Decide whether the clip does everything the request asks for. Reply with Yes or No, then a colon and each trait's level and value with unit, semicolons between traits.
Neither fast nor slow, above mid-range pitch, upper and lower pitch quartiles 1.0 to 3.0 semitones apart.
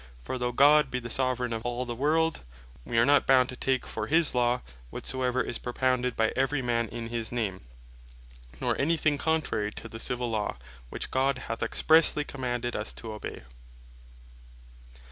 No: average, 175 wpm; low, 125 Hz; narrow, 2.5 semitones